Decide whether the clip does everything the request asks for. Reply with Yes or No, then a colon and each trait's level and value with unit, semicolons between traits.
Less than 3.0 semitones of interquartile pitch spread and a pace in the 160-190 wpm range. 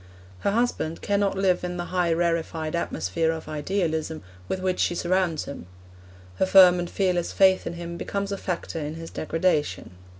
Yes: narrow, 2.6 semitones; average, 170 wpm